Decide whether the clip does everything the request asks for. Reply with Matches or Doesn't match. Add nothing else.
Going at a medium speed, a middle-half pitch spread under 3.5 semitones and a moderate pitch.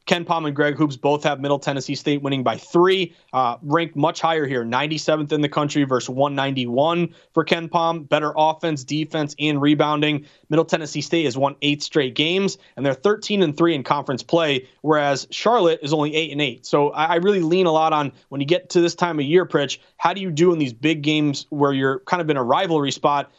Doesn't match